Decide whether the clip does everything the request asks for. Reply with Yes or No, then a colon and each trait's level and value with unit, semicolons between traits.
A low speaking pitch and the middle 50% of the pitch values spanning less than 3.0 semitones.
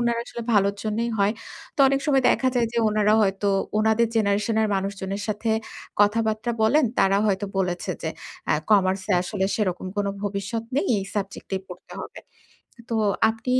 No: high, 210 Hz; narrow, 2.5 semitones